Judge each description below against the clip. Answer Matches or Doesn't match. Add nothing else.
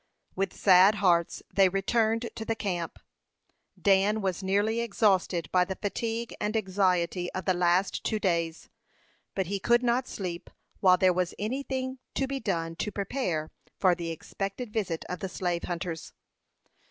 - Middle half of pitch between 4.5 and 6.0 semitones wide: Doesn't match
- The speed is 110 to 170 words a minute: Matches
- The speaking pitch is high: Matches